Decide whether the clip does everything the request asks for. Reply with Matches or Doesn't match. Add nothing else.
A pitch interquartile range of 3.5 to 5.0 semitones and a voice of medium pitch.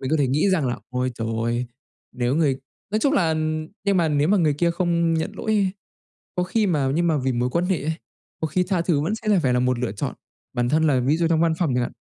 Doesn't match